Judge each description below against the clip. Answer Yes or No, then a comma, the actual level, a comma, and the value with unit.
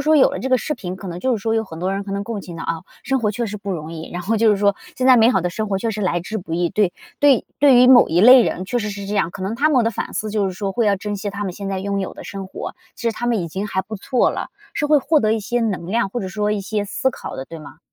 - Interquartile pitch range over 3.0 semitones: Yes, average, 3.5 semitones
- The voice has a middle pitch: No, high, 205 Hz